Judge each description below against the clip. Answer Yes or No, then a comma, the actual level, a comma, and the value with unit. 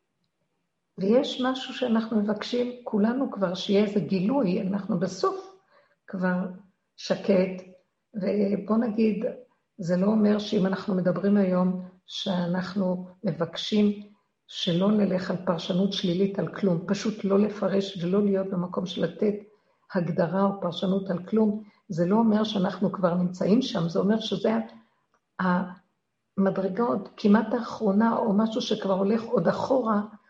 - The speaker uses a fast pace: No, average, 125 wpm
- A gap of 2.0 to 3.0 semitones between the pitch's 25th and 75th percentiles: Yes, average, 2.7 semitones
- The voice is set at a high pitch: Yes, high, 195 Hz